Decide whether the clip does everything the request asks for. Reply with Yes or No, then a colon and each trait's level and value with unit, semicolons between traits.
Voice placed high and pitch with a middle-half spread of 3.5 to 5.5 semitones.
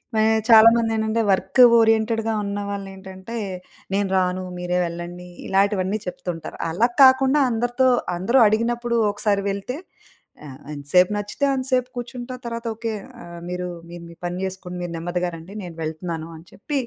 Yes: high, 200 Hz; average, 4.4 semitones